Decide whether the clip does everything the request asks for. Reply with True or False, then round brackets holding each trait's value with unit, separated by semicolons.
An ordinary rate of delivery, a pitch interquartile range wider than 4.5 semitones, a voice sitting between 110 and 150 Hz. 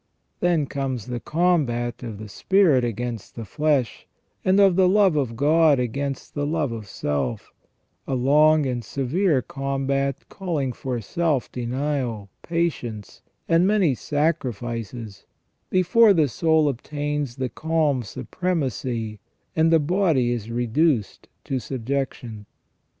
False (125 wpm; 5.0 semitones; 140 Hz)